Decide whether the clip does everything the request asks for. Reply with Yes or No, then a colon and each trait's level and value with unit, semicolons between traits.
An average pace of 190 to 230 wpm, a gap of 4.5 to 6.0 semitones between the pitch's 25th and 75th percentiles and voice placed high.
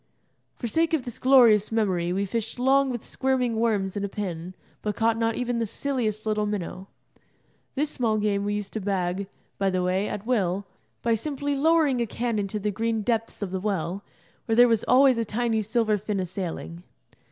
No: average, 200 wpm; average, 3.4 semitones; high, 215 Hz